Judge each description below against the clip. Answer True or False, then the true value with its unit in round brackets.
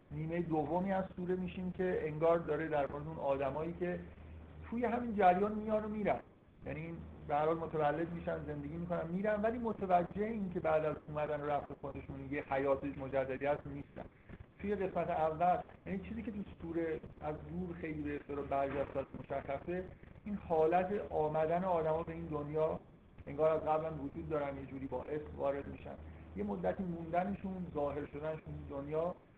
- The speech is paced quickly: True (165 wpm)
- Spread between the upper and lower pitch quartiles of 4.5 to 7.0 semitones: False (4.0 semitones)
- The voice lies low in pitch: False (155 Hz)